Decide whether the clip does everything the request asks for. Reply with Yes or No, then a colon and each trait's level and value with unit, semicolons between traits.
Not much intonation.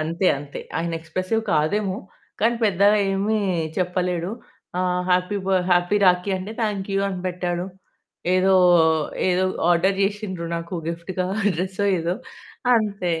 Yes: narrow, 2.0 semitones